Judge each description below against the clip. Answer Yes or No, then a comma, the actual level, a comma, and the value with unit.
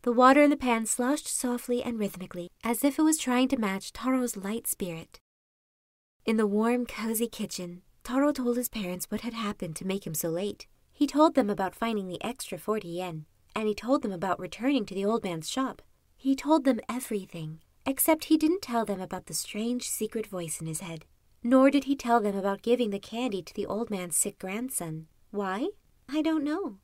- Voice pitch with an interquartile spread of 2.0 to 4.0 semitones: No, average, 5.1 semitones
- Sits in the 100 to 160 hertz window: No, high, 225 Hz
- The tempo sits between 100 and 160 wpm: No, fast, 205 wpm